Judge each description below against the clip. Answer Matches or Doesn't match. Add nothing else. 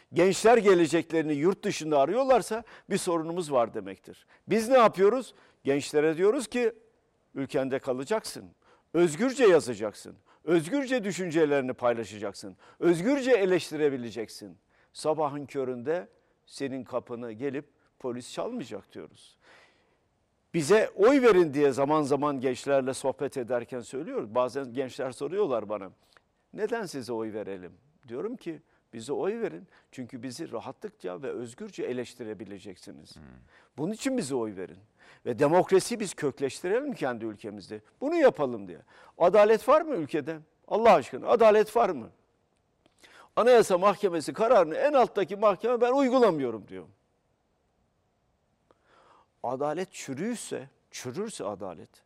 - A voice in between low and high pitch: Matches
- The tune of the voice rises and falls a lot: Matches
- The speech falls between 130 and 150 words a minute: Doesn't match